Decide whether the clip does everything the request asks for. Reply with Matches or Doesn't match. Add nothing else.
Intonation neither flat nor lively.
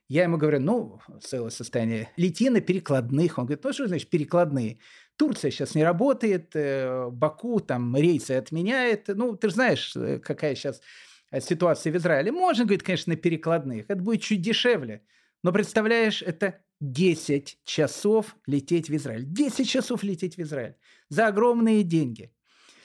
Doesn't match